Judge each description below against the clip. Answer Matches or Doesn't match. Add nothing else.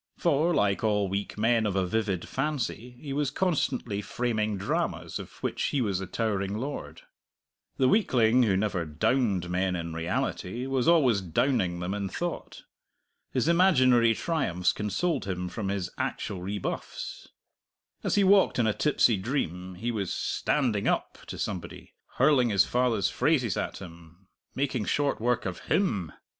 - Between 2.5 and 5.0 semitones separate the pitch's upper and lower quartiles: Doesn't match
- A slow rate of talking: Doesn't match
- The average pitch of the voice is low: Matches